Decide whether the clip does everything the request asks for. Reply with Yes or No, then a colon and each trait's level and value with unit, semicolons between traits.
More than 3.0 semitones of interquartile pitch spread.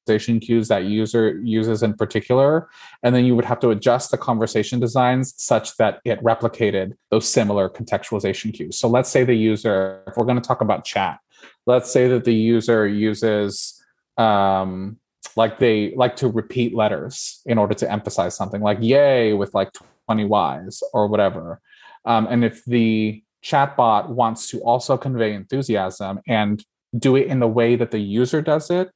No: narrow, 2.4 semitones